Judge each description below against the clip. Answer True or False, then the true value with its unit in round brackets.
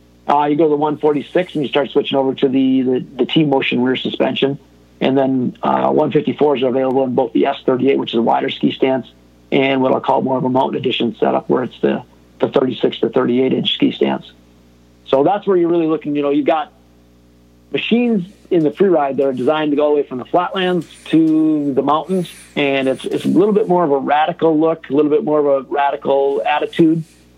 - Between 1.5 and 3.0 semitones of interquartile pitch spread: False (3.4 semitones)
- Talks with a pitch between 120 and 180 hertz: True (140 Hz)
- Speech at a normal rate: False (220 wpm)